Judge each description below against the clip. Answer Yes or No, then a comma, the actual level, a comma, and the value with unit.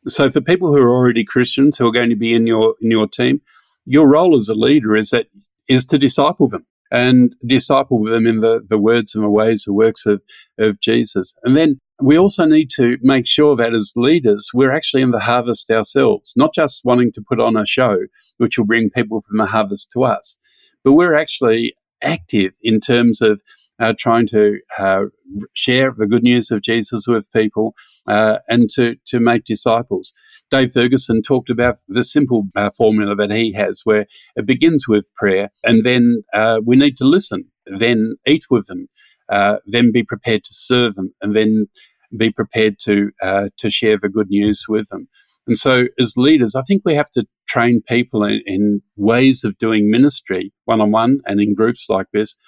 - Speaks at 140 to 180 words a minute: No, average, 200 wpm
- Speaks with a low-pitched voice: Yes, low, 115 Hz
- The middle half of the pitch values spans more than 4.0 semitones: No, average, 2.9 semitones